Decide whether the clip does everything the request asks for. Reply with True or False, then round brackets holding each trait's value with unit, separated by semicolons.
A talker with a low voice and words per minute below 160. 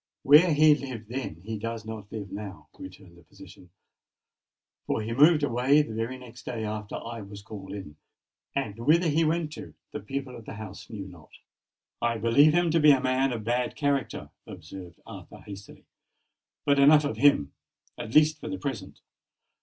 False (115 Hz; 175 wpm)